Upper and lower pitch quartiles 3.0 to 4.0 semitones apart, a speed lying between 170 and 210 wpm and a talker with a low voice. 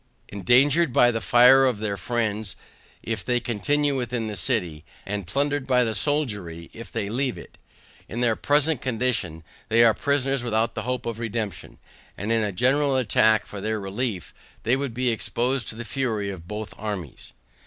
Yes: average, 3.7 semitones; average, 175 wpm; low, 115 Hz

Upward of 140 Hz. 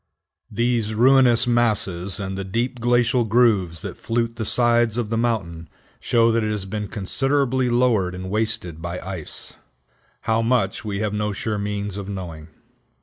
No: low, 110 Hz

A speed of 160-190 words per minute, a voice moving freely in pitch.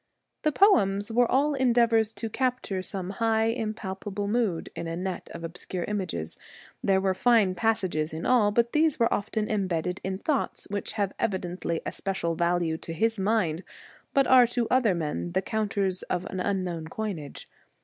No: average, 170 wpm; average, 4.1 semitones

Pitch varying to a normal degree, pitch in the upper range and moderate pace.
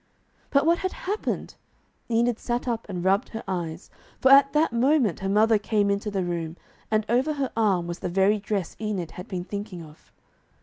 Yes: average, 4.7 semitones; high, 210 Hz; average, 190 wpm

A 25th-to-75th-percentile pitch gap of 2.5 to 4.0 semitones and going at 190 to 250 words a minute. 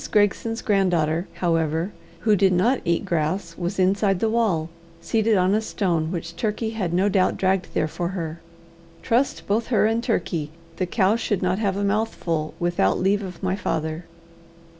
No: average, 3.7 semitones; average, 170 wpm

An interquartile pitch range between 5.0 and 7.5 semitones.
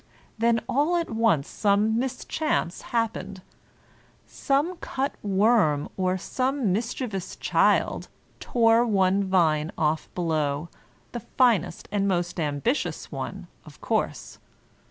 Yes: wide, 5.4 semitones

